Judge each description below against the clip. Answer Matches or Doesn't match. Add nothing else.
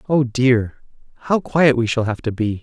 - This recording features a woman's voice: Doesn't match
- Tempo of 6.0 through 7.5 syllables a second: Doesn't match